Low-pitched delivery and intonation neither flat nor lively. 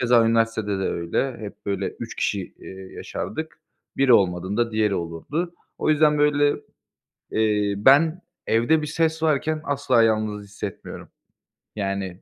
No: low, 115 Hz; wide, 6.4 semitones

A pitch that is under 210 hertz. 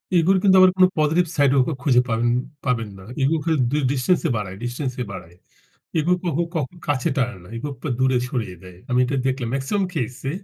Yes: low, 135 Hz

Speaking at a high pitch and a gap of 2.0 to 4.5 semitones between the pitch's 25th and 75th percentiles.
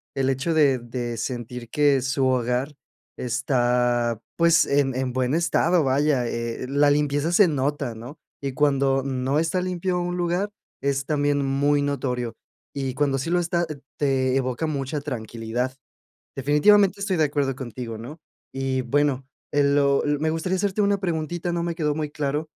No: medium, 140 Hz; average, 3.4 semitones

